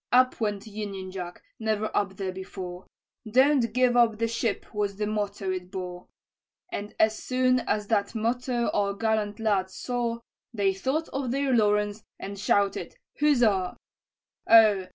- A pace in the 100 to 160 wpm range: Yes, average, 150 wpm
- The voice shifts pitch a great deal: No, average, 3.2 semitones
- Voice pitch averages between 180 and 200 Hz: No, high, 210 Hz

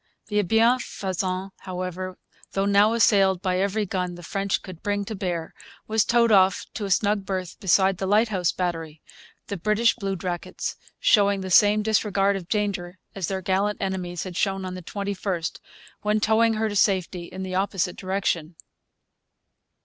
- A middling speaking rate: Yes, average, 160 wpm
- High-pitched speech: Yes, high, 195 Hz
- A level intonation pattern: Yes, narrow, 2.1 semitones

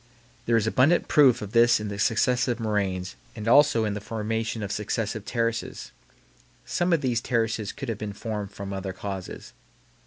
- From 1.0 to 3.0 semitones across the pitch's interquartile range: Yes, narrow, 2.5 semitones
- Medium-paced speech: Yes, average, 175 wpm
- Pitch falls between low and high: No, low, 110 Hz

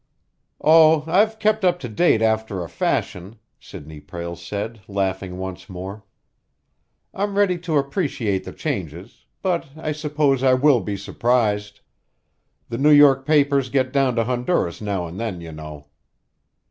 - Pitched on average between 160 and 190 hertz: No, low, 120 Hz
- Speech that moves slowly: No, average, 145 wpm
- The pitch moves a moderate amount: No, wide, 7.8 semitones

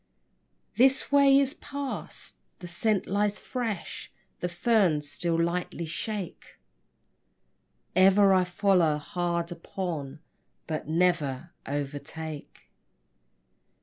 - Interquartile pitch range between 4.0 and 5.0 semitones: Yes, average, 4.3 semitones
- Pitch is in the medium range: Yes, medium, 175 Hz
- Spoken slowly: Yes, slow, 90 wpm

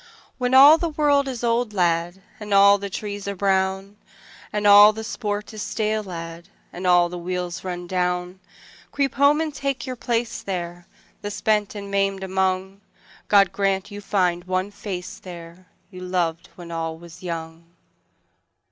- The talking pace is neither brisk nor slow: Yes, average, 165 wpm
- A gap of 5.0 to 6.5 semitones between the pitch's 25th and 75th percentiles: No, average, 3.0 semitones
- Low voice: No, high, 195 Hz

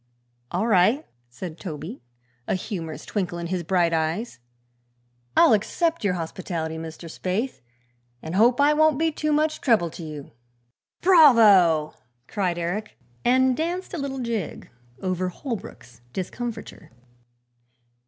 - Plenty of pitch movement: Yes, wide, 7.3 semitones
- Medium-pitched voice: No, high, 195 Hz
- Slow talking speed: Yes, slow, 125 wpm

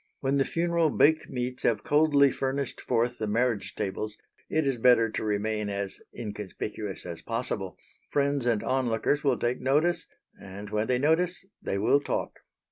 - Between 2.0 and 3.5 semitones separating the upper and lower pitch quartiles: No, average, 4.9 semitones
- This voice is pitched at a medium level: No, low, 125 Hz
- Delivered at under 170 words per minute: Yes, average, 160 wpm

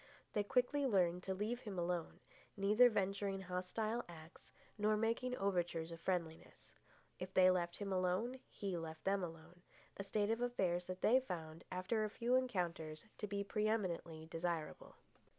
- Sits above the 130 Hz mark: Yes, high, 190 Hz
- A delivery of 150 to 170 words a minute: Yes, average, 155 wpm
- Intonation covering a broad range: No, average, 3.7 semitones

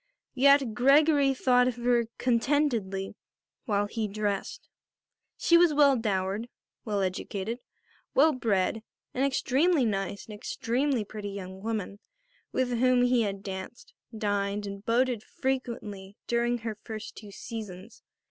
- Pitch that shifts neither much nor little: Yes, average, 4.1 semitones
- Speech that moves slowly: Yes, slow, 130 wpm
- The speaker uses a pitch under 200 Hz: No, high, 225 Hz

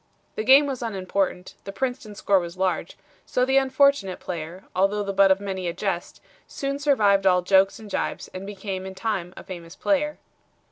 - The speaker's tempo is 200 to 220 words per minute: No, average, 185 wpm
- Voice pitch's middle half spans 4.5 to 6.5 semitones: No, average, 4.1 semitones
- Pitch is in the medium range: No, high, 195 Hz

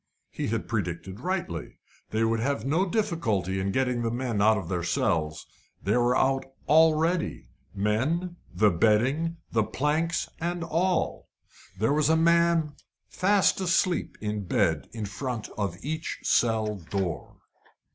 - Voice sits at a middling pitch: No, low, 120 Hz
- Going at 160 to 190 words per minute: No, average, 140 wpm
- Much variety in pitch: Yes, wide, 7.9 semitones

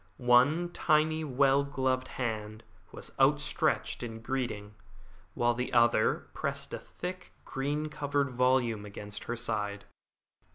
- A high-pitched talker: No, low, 125 Hz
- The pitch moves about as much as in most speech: Yes, average, 3.9 semitones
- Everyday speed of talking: No, slow, 120 wpm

